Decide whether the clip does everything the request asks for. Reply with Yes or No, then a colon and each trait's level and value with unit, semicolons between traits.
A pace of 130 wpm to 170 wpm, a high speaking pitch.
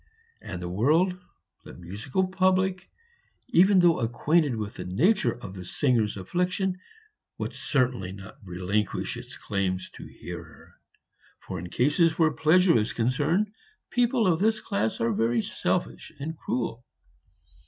No: average, 140 wpm; low, 130 Hz